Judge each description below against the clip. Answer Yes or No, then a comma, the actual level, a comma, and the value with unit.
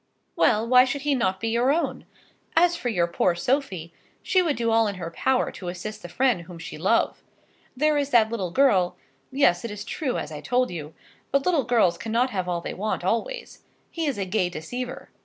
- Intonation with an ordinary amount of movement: No, wide, 6.7 semitones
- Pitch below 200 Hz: No, high, 225 Hz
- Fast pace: Yes, fast, 215 wpm